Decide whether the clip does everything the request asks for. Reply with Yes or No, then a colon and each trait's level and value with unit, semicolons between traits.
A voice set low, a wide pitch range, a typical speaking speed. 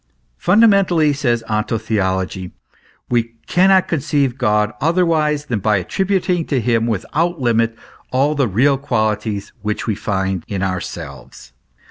No: low, 120 Hz; wide, 6.4 semitones; slow, 130 wpm